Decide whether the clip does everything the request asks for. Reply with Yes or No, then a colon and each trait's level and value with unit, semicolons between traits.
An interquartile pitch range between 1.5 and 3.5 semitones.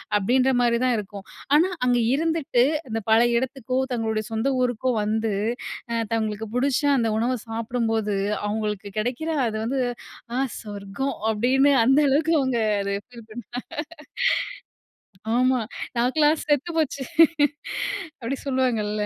Yes: average, 3.2 semitones